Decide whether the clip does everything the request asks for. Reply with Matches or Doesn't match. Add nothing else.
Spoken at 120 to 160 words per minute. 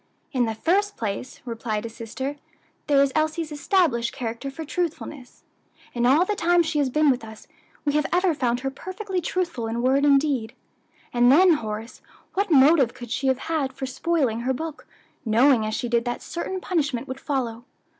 Doesn't match